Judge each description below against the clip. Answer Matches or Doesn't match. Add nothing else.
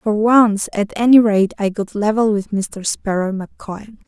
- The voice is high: Matches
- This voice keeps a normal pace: Matches